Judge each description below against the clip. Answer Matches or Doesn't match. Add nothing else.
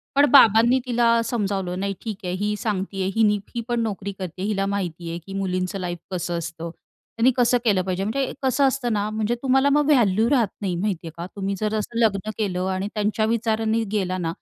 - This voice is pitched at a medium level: Doesn't match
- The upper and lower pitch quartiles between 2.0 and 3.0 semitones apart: Doesn't match